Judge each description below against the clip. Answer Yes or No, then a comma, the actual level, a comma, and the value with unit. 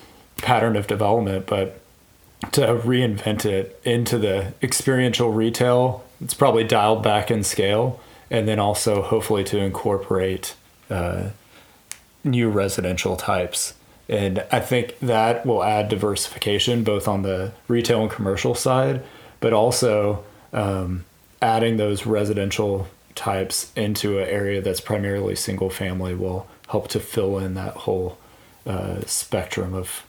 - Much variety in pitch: No, average, 3.2 semitones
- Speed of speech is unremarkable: No, slow, 130 wpm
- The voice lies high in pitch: No, low, 105 Hz